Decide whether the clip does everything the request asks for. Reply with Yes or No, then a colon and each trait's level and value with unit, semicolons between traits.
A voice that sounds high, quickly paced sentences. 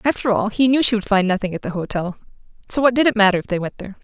Yes: high, 210 Hz; fast, 285 wpm